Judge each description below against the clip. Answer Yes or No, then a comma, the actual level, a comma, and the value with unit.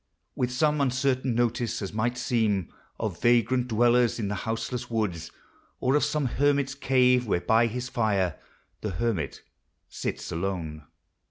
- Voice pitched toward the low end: Yes, low, 120 Hz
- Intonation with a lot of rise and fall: No, average, 3.3 semitones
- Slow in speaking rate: No, average, 145 wpm